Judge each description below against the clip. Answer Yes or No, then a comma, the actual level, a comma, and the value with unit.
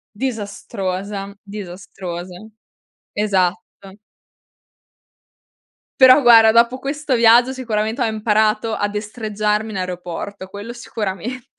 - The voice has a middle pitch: No, high, 215 Hz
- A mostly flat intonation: No, average, 3.0 semitones